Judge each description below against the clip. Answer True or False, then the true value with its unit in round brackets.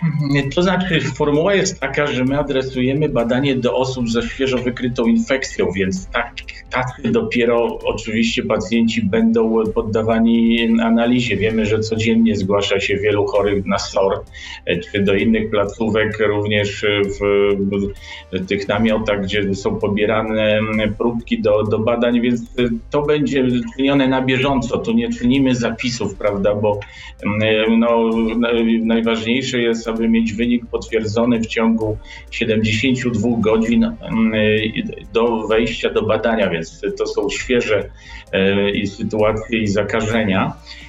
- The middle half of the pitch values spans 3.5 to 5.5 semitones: False (3.1 semitones)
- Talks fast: False (125 wpm)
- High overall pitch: False (115 Hz)